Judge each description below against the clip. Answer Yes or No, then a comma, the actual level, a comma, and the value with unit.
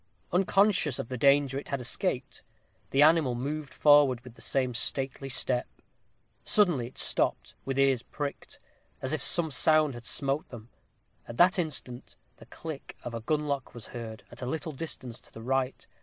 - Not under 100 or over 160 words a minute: No, average, 175 wpm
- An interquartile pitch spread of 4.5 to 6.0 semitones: No, average, 3.4 semitones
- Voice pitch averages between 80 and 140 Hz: Yes, low, 135 Hz